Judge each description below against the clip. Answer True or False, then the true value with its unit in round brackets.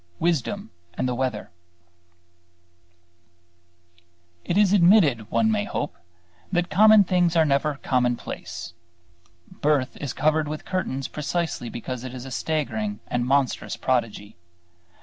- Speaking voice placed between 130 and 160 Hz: True (140 Hz)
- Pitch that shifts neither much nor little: False (5.7 semitones)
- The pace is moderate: False (120 wpm)